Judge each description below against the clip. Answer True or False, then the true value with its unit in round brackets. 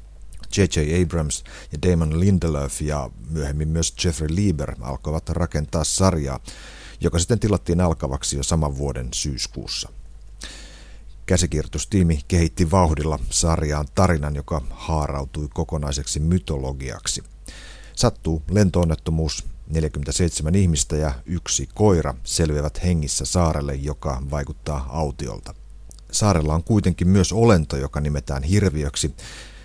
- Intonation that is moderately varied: True (3.3 semitones)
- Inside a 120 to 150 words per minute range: False (105 wpm)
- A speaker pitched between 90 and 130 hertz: False (80 Hz)